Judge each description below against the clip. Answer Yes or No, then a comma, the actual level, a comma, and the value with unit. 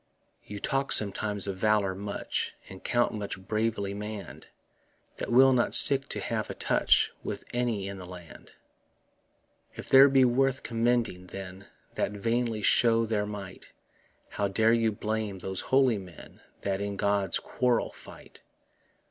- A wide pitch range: No, average, 3.3 semitones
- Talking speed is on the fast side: No, average, 150 wpm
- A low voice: Yes, low, 105 Hz